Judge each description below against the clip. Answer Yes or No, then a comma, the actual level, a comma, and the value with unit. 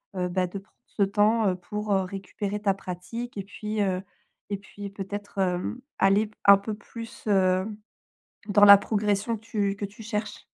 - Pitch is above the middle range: Yes, high, 200 Hz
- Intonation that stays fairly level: Yes, narrow, 1.5 semitones